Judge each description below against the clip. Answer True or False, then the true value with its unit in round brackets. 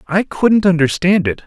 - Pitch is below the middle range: False (175 Hz)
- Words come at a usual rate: True (165 wpm)